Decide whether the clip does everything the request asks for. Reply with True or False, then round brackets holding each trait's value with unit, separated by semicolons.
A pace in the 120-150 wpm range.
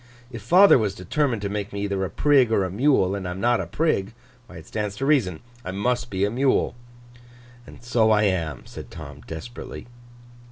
False (205 wpm)